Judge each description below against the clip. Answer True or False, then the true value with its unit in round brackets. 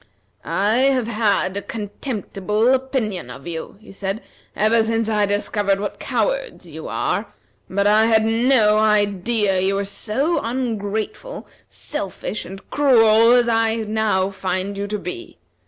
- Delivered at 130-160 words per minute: True (145 wpm)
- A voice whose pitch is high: True (215 Hz)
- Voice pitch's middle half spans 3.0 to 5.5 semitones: False (2.6 semitones)